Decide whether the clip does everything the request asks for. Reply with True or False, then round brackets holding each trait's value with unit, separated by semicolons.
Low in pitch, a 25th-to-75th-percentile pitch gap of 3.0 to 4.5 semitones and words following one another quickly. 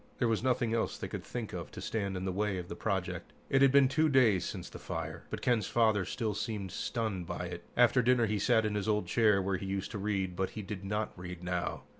True (105 Hz; 3.5 semitones; 255 wpm)